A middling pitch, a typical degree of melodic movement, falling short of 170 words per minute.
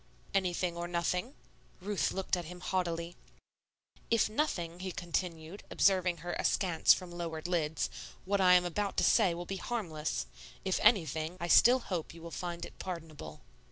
No: medium, 175 Hz; narrow, 2.1 semitones; average, 160 wpm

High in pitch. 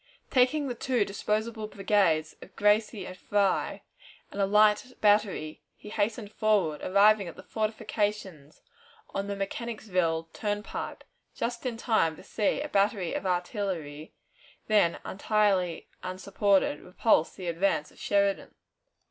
Yes: high, 200 Hz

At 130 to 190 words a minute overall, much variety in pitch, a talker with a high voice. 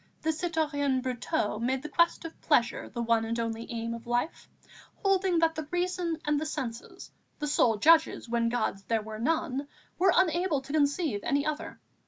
Yes: average, 180 wpm; wide, 5.8 semitones; very high, 285 Hz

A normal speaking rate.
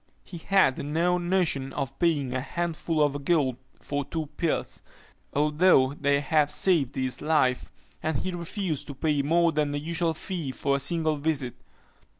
Yes: average, 160 wpm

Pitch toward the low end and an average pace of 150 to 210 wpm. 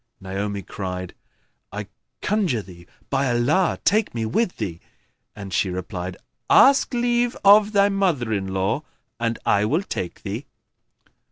No: low, 115 Hz; average, 140 wpm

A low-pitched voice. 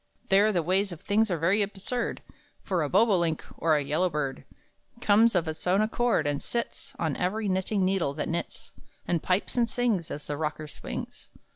No: medium, 185 Hz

